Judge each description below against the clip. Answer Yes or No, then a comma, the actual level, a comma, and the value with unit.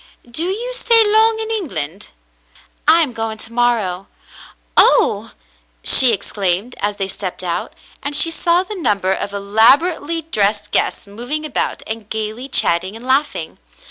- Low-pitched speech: No, high, 225 Hz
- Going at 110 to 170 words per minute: Yes, average, 150 wpm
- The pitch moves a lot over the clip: Yes, wide, 8.4 semitones